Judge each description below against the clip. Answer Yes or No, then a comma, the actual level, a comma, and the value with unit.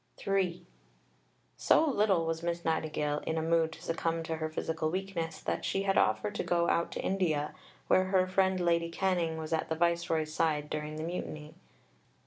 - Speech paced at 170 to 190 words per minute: Yes, average, 180 wpm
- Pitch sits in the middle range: Yes, medium, 165 Hz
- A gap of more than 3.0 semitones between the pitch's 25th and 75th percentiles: No, narrow, 2.5 semitones